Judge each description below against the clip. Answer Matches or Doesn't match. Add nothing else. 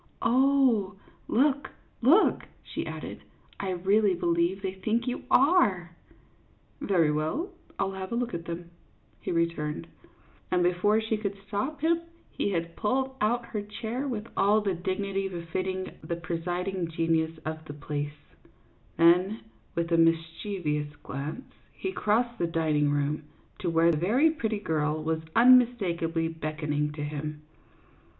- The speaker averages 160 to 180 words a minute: Doesn't match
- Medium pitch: Matches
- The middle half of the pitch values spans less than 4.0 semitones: Doesn't match